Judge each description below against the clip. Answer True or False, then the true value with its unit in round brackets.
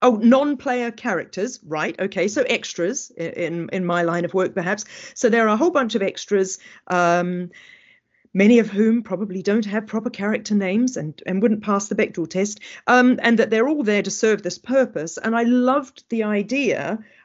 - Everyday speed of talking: True (190 wpm)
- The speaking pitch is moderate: False (215 Hz)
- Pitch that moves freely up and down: False (4.3 semitones)